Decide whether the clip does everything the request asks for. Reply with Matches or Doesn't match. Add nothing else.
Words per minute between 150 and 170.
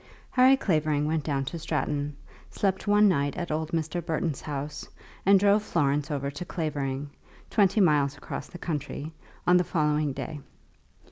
Matches